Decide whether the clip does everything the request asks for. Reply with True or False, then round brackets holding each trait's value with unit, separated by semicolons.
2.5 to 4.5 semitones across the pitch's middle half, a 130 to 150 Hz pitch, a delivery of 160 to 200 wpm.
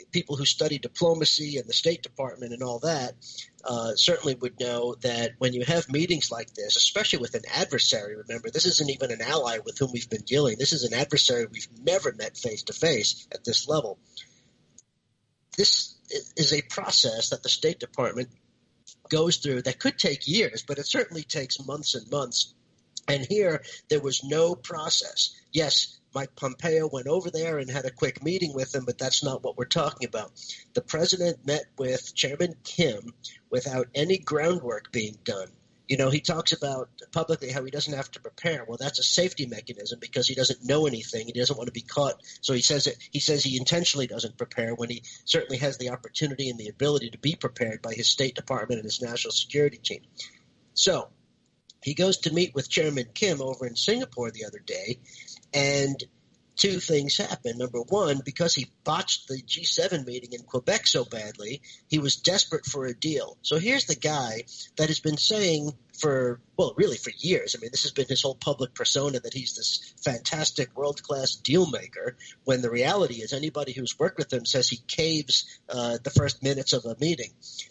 True (4.0 semitones; 135 Hz; 195 wpm)